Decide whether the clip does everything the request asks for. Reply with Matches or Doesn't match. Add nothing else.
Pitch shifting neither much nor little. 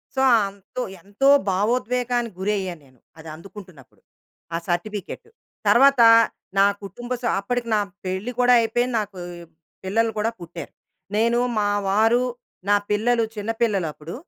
Matches